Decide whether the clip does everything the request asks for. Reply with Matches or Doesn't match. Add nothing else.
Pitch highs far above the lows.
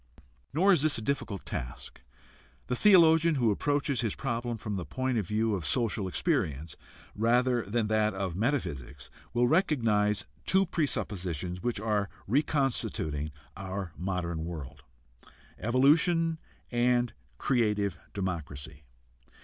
Matches